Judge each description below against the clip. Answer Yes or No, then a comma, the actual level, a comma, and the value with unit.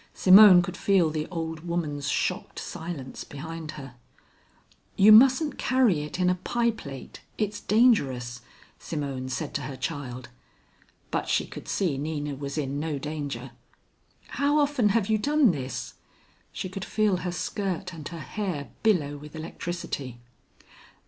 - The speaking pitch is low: No, medium, 165 Hz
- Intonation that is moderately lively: No, wide, 5.9 semitones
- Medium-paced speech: Yes, average, 145 wpm